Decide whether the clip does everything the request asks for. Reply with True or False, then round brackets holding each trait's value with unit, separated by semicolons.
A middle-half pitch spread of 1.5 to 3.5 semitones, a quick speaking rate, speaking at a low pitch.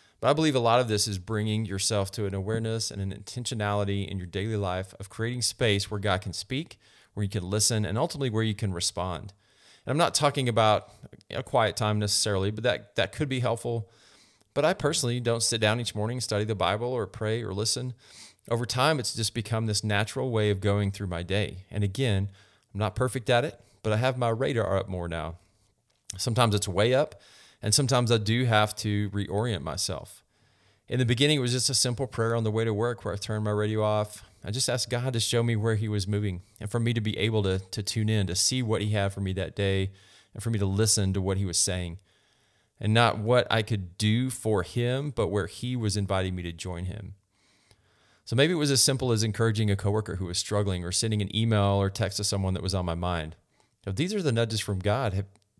True (2.8 semitones; 235 wpm; 105 Hz)